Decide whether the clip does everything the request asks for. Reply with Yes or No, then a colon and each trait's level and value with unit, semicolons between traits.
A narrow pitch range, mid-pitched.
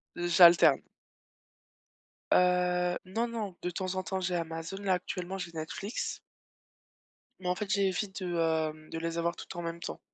Yes: narrow, 2.0 semitones; medium, 180 Hz